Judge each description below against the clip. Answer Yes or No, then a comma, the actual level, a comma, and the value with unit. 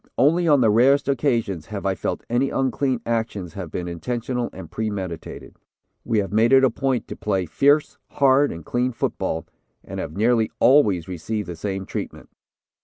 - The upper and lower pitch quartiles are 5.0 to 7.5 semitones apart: Yes, wide, 5.5 semitones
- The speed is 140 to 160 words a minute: No, average, 175 wpm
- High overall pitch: No, low, 115 Hz